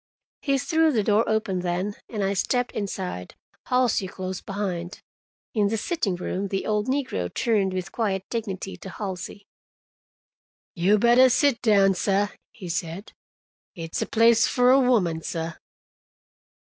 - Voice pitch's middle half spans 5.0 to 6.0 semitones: No, average, 4.0 semitones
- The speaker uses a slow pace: No, average, 145 wpm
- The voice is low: No, high, 205 Hz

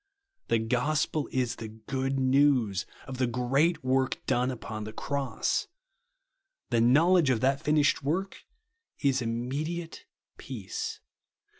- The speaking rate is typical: No, slow, 120 wpm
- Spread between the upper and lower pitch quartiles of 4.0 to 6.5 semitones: No, average, 3.2 semitones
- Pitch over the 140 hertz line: No, low, 130 Hz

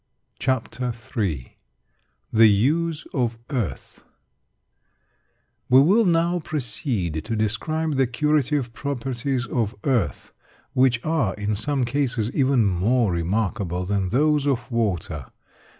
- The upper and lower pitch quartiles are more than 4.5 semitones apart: Yes, average, 5.2 semitones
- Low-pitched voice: Yes, low, 120 Hz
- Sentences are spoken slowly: Yes, slow, 110 wpm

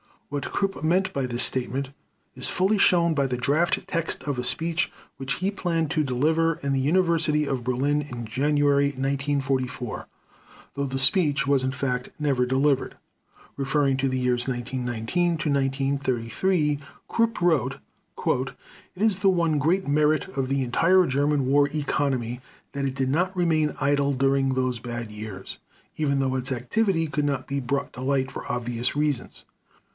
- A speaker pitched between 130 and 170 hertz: Yes, medium, 140 Hz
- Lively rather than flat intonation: No, average, 3.2 semitones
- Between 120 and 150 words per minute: No, average, 160 wpm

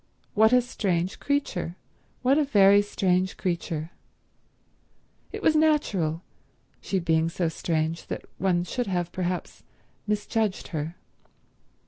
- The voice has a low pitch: No, medium, 185 Hz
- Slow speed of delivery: Yes, slow, 115 wpm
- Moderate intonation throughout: Yes, average, 4.5 semitones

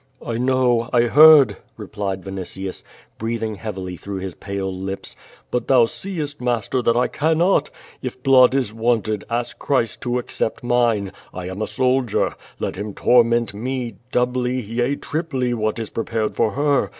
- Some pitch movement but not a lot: Yes, average, 3.5 semitones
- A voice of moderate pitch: No, low, 120 Hz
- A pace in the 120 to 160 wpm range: Yes, average, 155 wpm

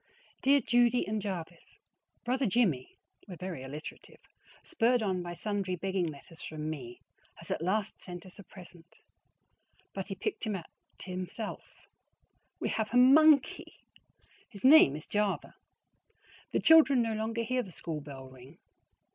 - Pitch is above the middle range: Yes, high, 195 Hz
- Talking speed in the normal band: Yes, average, 150 wpm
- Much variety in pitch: Yes, wide, 6.1 semitones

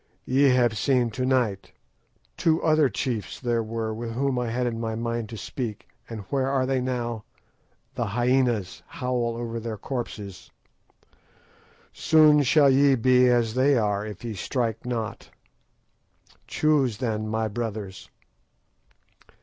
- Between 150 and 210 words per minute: No, average, 140 wpm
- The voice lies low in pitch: Yes, low, 120 Hz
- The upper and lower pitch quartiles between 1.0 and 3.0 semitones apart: Yes, average, 2.7 semitones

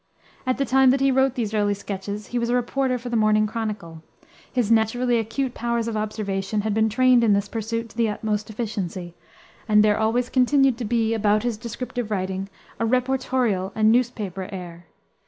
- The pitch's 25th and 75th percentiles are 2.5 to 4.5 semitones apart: Yes, average, 2.9 semitones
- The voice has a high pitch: Yes, high, 220 Hz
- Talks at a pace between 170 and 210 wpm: Yes, average, 190 wpm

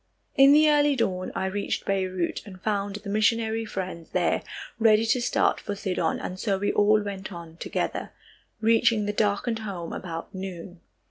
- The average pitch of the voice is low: No, high, 205 Hz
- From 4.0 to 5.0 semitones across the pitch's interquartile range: No, average, 3.0 semitones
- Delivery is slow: No, average, 165 wpm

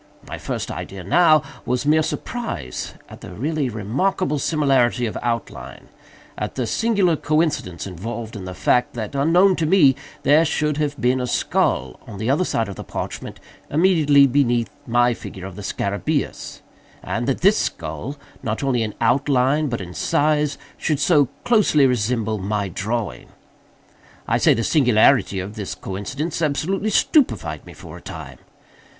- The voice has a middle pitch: No, low, 130 Hz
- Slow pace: No, average, 155 wpm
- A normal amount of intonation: No, wide, 5.8 semitones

